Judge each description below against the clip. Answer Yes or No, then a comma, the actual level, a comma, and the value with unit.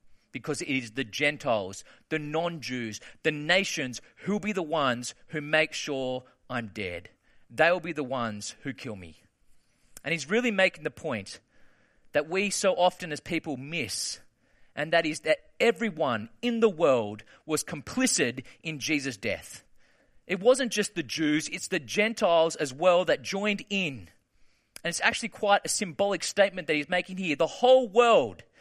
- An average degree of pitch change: No, wide, 6.3 semitones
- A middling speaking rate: Yes, average, 170 wpm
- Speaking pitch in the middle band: Yes, medium, 160 Hz